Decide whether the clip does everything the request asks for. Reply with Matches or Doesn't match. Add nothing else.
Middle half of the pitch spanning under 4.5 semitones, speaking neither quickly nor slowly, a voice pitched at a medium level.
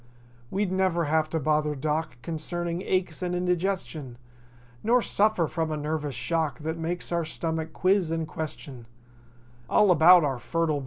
Matches